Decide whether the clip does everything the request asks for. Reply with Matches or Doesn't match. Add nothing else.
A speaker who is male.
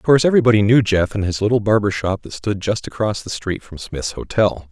Matches